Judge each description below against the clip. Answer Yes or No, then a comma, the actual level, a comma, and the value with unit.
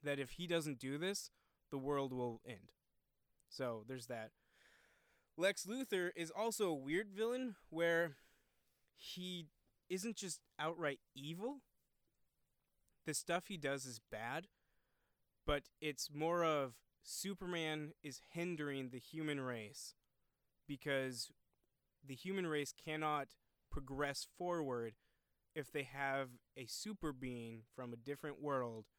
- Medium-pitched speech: Yes, medium, 150 Hz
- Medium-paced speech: No, slow, 120 wpm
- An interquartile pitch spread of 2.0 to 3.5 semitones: No, average, 4.5 semitones